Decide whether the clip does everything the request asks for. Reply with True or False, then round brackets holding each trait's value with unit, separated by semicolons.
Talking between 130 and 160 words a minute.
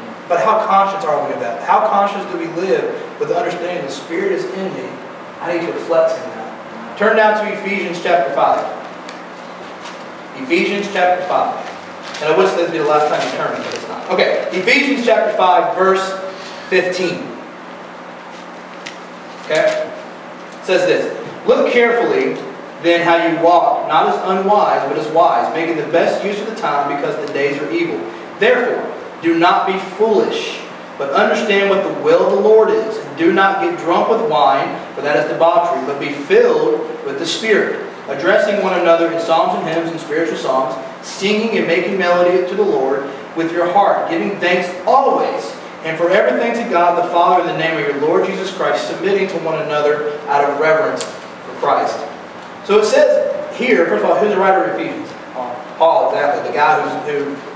False (190 wpm)